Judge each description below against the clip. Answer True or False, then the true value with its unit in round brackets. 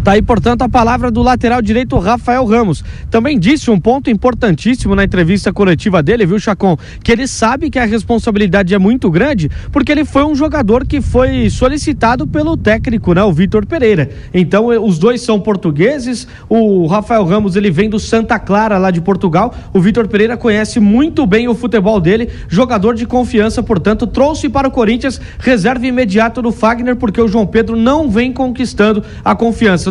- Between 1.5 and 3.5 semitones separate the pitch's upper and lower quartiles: True (3.1 semitones)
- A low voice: False (225 Hz)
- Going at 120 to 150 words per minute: False (180 wpm)